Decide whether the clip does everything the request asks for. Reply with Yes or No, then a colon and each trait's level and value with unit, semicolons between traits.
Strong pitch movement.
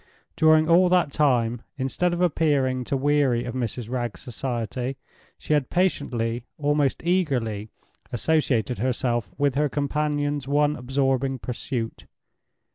No: average, 3.4 semitones